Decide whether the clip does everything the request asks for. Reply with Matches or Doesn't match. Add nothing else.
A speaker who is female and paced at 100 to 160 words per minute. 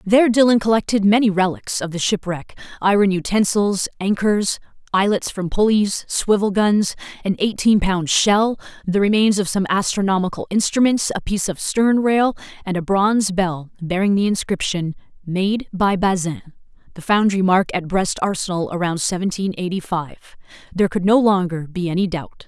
Matches